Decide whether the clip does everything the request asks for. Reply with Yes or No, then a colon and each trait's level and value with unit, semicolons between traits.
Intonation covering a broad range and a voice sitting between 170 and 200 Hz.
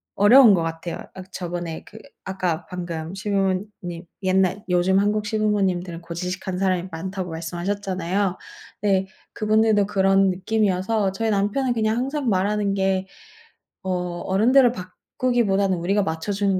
No: narrow, 2.5 semitones; high, 190 Hz